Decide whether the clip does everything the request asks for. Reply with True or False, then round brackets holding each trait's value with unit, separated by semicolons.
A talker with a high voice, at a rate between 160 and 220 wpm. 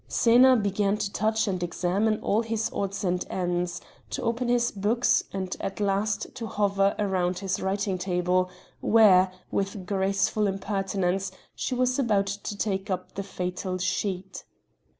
False (195 Hz; 150 wpm)